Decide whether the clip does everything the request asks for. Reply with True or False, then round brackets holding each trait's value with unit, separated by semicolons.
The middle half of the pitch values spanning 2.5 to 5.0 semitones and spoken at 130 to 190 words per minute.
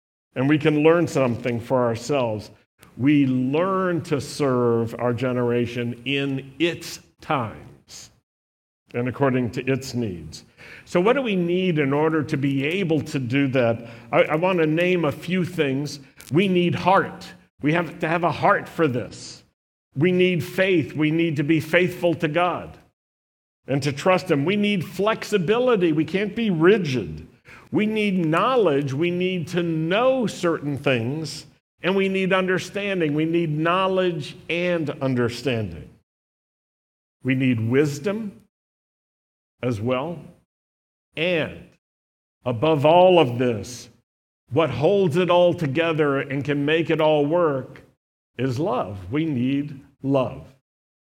False (5.6 semitones; 140 wpm)